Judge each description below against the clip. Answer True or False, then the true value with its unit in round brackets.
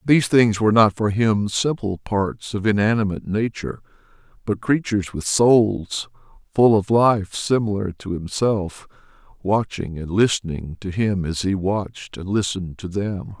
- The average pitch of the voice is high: False (100 Hz)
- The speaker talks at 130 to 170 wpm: True (150 wpm)